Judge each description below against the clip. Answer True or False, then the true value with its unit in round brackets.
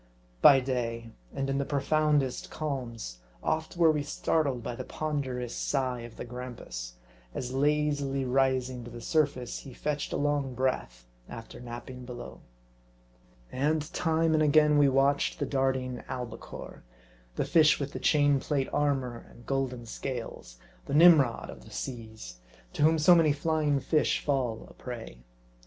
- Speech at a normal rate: True (155 wpm)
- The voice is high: False (135 Hz)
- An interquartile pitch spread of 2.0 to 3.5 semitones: True (3.2 semitones)